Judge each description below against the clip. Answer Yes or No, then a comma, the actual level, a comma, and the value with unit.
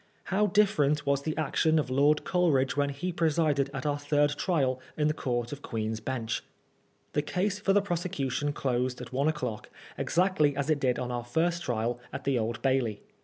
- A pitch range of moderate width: Yes, average, 3.8 semitones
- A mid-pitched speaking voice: Yes, medium, 145 Hz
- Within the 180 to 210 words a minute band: Yes, average, 190 wpm